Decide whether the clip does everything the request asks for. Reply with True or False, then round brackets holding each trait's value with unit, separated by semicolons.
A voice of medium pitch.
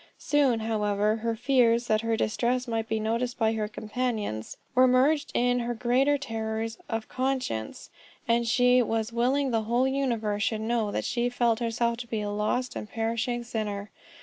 False (230 Hz)